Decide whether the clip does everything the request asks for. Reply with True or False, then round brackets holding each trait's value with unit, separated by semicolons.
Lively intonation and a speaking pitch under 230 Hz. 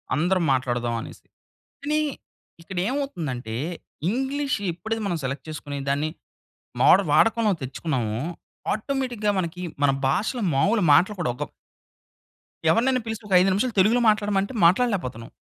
True (8.1 semitones; 190 Hz)